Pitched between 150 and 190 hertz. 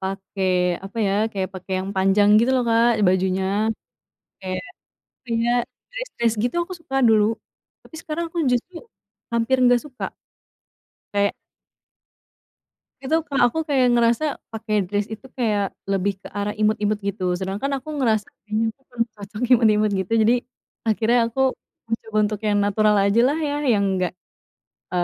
No: high, 215 Hz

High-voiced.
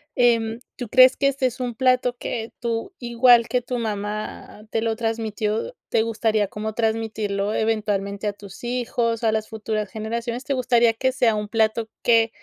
Yes: high, 225 Hz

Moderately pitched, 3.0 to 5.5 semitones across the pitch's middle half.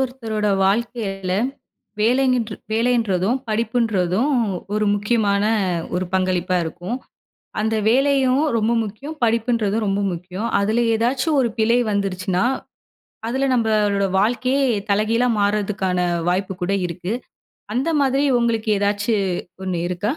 No: high, 215 Hz; average, 3.5 semitones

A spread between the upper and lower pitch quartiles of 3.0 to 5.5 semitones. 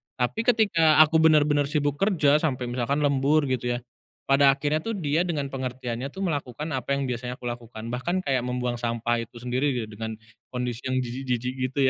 Yes: average, 3.4 semitones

